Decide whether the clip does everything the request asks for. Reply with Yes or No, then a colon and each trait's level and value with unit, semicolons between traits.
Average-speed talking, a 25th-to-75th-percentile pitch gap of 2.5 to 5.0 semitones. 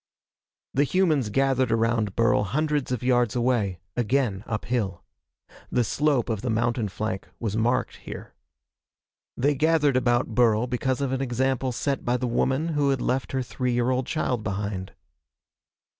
Yes: average, 155 wpm; average, 3.0 semitones